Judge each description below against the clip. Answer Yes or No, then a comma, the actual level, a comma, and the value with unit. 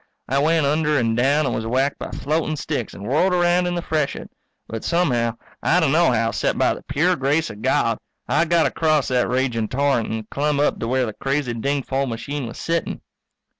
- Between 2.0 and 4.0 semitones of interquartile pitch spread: No, average, 4.4 semitones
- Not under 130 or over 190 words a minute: No, fast, 205 wpm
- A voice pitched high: No, medium, 140 Hz